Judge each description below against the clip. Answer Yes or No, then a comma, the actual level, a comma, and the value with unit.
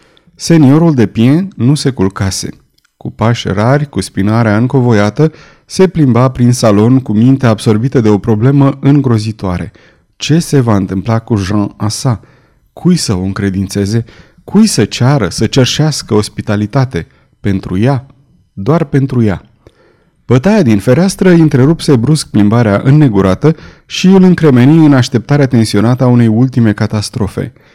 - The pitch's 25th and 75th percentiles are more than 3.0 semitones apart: Yes, average, 5.2 semitones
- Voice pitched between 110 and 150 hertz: Yes, low, 120 Hz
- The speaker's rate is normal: Yes, average, 135 wpm